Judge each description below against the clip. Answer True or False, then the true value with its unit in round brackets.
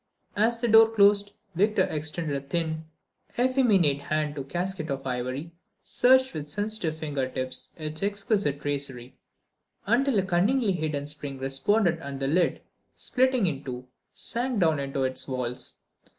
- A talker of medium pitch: True (160 Hz)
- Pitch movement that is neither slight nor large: False (6.8 semitones)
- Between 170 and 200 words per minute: False (150 wpm)